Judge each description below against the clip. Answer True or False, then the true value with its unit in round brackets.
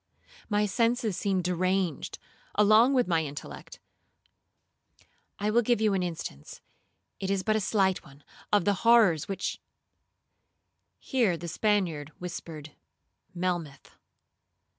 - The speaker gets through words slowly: True (120 wpm)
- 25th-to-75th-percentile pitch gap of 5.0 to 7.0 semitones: False (3.9 semitones)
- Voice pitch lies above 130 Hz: True (190 Hz)